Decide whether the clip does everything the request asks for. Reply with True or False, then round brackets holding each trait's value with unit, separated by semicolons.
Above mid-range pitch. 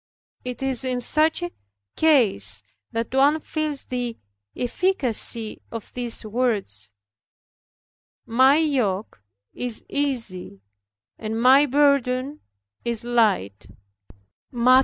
True (245 Hz)